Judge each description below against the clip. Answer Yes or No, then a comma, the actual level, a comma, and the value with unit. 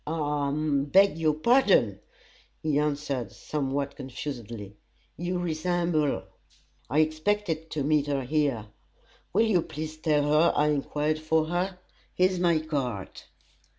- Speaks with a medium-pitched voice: Yes, medium, 155 Hz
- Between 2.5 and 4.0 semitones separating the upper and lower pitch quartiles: Yes, average, 2.9 semitones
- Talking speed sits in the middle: No, slow, 130 wpm